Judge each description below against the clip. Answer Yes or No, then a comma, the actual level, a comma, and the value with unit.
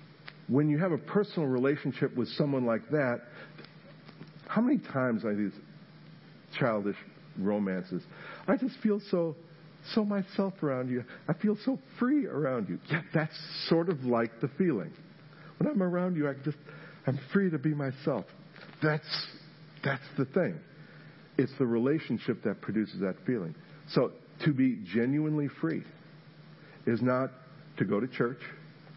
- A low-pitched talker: No, medium, 155 Hz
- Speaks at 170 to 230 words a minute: No, average, 145 wpm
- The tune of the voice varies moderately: Yes, average, 3.8 semitones